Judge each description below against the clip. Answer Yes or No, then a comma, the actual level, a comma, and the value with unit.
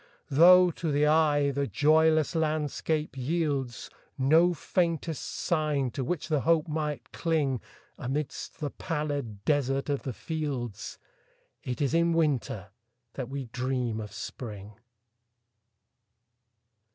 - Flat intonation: No, average, 3.5 semitones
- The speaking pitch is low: No, medium, 145 Hz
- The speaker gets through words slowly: Yes, slow, 105 wpm